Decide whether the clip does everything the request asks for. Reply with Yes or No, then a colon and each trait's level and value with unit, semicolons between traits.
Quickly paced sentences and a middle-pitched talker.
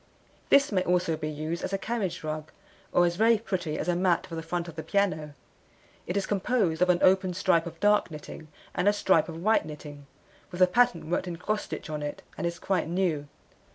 Yes: fast, 225 wpm; medium, 175 Hz